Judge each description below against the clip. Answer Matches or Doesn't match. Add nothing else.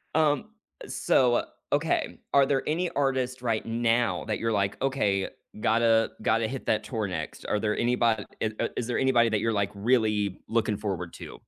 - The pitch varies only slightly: Doesn't match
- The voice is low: Matches